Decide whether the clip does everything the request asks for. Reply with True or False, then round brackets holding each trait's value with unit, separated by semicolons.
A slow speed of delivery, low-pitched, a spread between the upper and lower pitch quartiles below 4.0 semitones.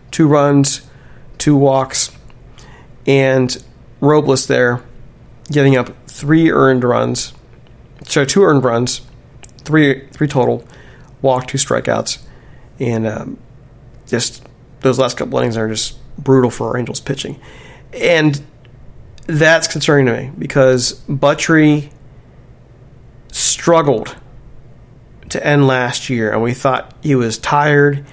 True (115 wpm; 130 Hz; 2.4 semitones)